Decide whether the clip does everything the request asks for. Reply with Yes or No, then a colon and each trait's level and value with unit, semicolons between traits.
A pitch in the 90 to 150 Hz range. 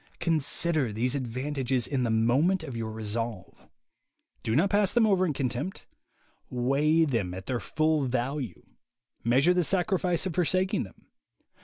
Yes: medium, 140 Hz